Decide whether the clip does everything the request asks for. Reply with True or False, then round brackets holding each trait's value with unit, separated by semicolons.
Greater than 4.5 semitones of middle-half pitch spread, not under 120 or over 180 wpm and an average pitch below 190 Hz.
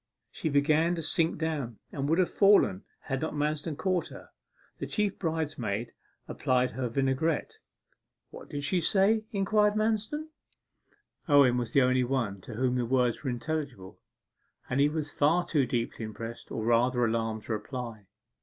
True (5.1 semitones; 160 wpm; 140 Hz)